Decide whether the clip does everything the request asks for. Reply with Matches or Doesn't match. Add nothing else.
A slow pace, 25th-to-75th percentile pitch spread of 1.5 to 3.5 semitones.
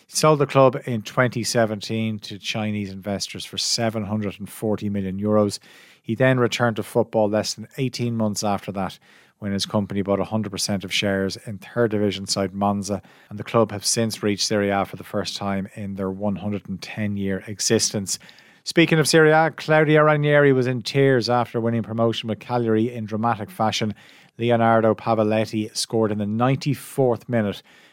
Doesn't match